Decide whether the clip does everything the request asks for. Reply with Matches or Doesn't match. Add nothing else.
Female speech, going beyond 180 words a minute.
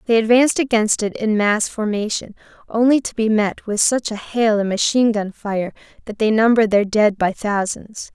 Matches